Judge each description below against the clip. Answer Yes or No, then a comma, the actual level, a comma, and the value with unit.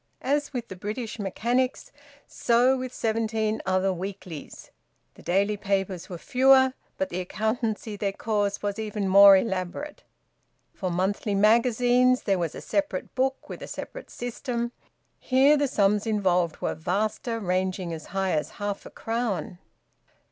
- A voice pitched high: Yes, high, 210 Hz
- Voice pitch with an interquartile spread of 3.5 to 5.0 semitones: Yes, average, 4.2 semitones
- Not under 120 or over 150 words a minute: Yes, average, 145 wpm